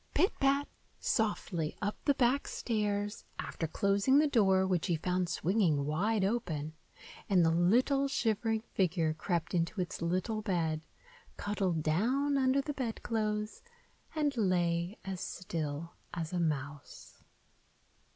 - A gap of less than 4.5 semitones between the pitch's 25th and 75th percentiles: No, average, 5.1 semitones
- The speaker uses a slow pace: Yes, slow, 130 wpm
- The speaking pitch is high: Yes, high, 195 Hz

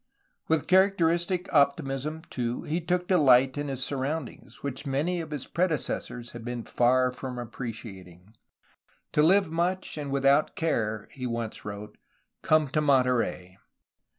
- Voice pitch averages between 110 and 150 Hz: Yes, low, 135 Hz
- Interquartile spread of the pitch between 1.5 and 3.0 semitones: No, average, 4.8 semitones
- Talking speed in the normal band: Yes, average, 150 wpm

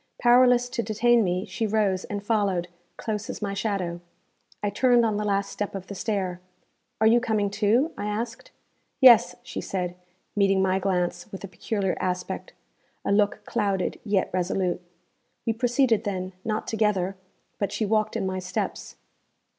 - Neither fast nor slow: Yes, average, 160 wpm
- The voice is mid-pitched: No, high, 205 Hz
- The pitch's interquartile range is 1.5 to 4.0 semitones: Yes, average, 2.8 semitones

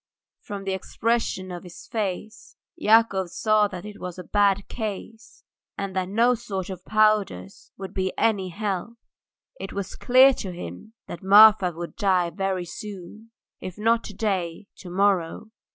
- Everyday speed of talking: Yes, average, 155 wpm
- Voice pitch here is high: Yes, high, 195 Hz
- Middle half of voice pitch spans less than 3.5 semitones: Yes, average, 2.9 semitones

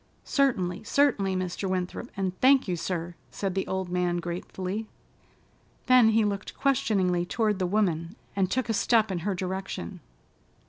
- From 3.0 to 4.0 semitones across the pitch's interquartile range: Yes, average, 3.4 semitones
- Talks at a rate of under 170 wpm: Yes, average, 150 wpm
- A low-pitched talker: No, high, 190 Hz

